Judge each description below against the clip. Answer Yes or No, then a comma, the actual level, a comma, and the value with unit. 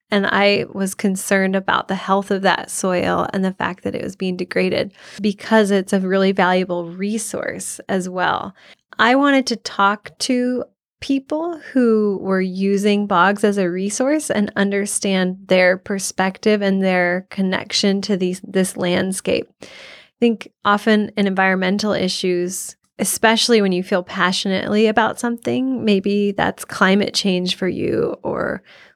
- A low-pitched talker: No, high, 200 Hz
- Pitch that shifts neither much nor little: No, narrow, 2.3 semitones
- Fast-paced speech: No, average, 145 wpm